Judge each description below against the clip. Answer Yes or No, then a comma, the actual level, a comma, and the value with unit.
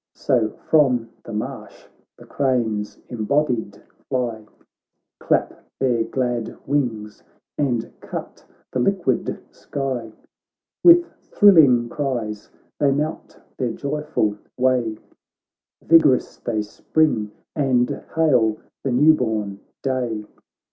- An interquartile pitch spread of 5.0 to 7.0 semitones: No, average, 4.2 semitones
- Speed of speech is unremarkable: No, slow, 100 wpm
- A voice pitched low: Yes, low, 125 Hz